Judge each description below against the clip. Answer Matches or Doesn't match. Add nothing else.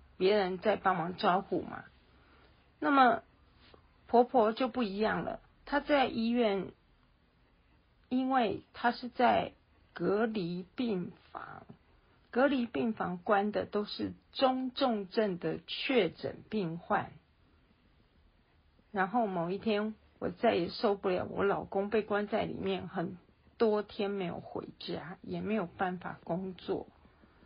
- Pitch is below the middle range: Doesn't match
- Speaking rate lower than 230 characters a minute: Matches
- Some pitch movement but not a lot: Matches